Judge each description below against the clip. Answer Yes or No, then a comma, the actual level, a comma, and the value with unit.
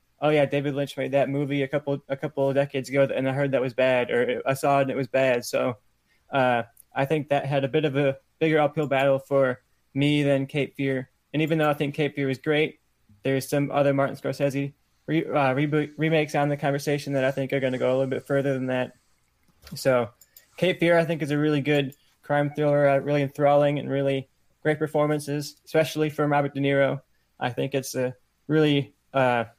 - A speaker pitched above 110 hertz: Yes, medium, 140 Hz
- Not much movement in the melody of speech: Yes, narrow, 1.6 semitones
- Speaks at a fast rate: Yes, fast, 220 wpm